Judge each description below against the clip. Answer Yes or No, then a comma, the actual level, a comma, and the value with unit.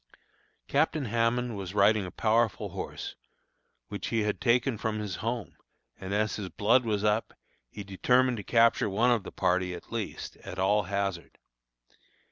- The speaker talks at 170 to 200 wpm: No, average, 160 wpm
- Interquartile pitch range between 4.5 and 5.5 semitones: No, average, 2.8 semitones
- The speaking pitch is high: No, low, 105 Hz